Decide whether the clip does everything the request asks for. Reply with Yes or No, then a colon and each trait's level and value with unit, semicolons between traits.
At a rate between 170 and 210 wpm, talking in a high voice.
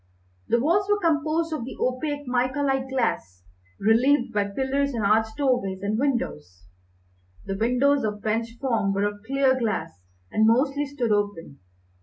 No: average, 155 wpm; high, 245 Hz